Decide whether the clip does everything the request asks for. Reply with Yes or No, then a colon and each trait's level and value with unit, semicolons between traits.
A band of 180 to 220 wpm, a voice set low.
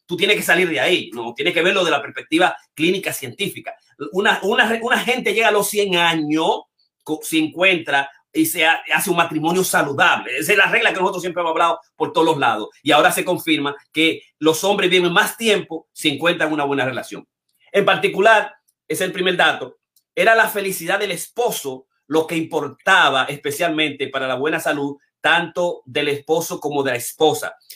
No: fast, 190 wpm; medium, 170 Hz